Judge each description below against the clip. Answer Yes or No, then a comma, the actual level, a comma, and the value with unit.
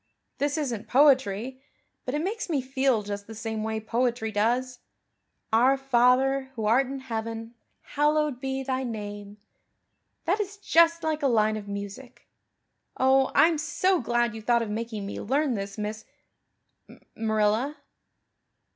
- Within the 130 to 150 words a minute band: Yes, average, 145 wpm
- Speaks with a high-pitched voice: Yes, high, 245 Hz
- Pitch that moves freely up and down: No, average, 3.8 semitones